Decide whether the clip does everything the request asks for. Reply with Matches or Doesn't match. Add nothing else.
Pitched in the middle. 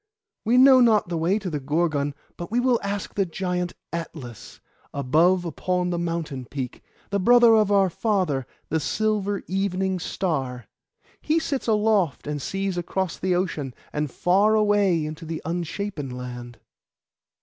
Matches